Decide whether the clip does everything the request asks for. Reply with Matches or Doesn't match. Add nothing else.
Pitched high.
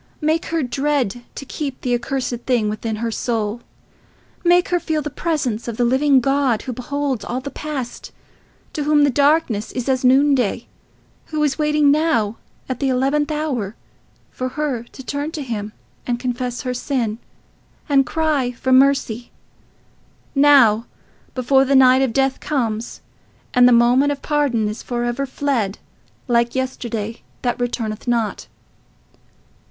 Matches